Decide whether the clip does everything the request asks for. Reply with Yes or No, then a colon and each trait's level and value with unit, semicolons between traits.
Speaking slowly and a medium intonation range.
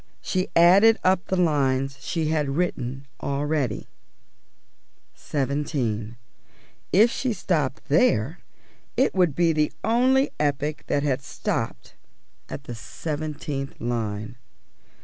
Yes: slow, 110 wpm; average, 4.7 semitones